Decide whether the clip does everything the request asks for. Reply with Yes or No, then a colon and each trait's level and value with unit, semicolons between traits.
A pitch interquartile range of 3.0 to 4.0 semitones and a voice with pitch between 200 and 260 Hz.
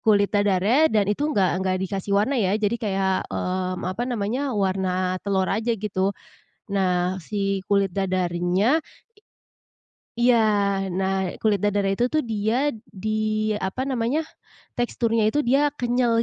Yes: average, 3.6 semitones; high, 205 Hz